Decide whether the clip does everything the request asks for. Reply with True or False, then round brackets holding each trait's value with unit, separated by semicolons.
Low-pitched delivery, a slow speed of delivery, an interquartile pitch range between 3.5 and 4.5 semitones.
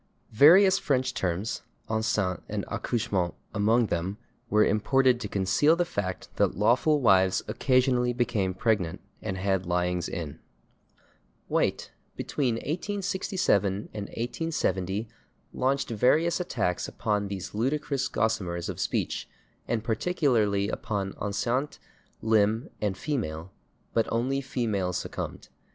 False (110 Hz; 115 wpm; 5.2 semitones)